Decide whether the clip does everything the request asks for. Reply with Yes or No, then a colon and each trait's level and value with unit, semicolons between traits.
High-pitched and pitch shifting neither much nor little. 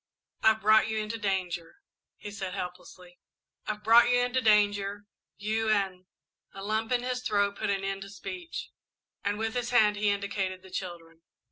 No: high, 205 Hz; narrow, 2.3 semitones